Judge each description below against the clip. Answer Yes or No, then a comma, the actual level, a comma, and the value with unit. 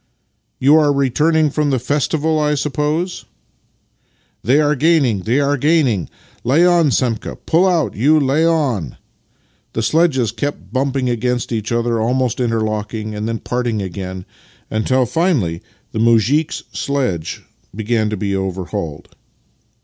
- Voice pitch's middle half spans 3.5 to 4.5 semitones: No, wide, 5.4 semitones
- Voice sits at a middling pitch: No, low, 125 Hz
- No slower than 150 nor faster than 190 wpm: No, average, 140 wpm